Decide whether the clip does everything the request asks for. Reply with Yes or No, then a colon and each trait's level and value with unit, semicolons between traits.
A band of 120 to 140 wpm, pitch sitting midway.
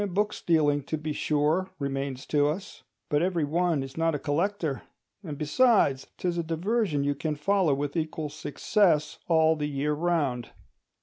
No: average, 165 wpm; medium, 155 Hz